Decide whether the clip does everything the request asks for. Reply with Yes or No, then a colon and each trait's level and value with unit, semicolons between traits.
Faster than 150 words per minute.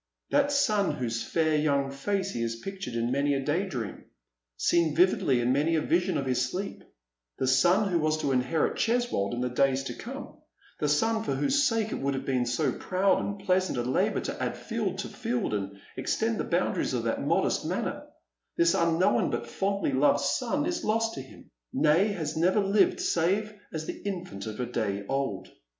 Yes: fast, 205 wpm